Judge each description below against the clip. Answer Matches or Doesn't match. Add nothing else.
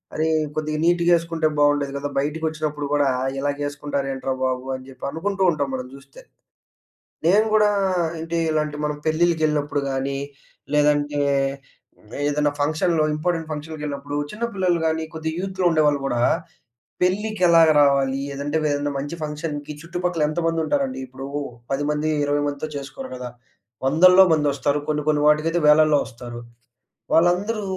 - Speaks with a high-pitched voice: Doesn't match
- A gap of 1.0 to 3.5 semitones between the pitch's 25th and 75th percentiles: Matches